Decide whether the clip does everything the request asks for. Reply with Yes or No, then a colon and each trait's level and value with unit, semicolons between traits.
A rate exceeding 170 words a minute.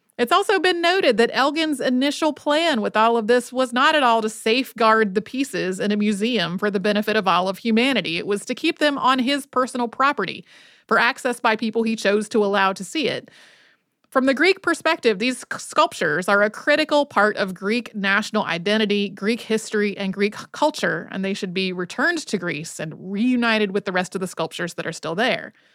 Yes: fast, 205 wpm